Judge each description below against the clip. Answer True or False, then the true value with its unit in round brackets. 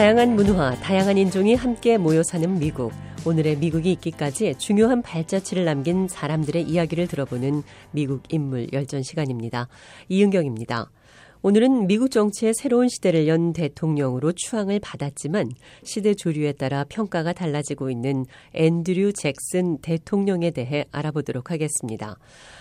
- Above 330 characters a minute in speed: True (350 characters per minute)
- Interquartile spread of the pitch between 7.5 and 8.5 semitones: False (5.4 semitones)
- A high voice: False (165 Hz)